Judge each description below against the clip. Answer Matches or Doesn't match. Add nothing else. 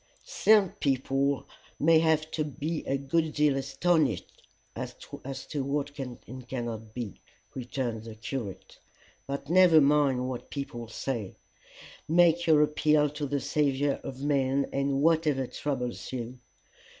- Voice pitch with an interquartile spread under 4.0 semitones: Matches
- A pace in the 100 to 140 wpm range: Matches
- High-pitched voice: Doesn't match